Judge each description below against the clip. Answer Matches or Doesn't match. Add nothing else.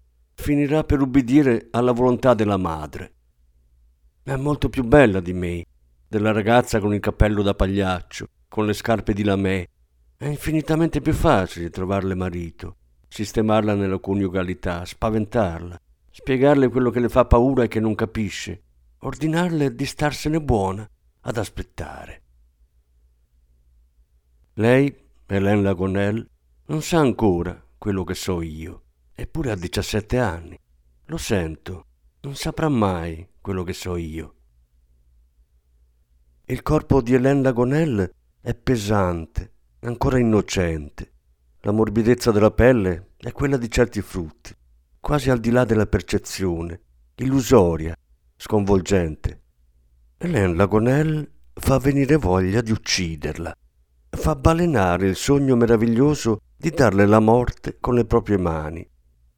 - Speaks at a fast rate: Doesn't match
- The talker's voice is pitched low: Matches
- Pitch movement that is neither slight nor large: Doesn't match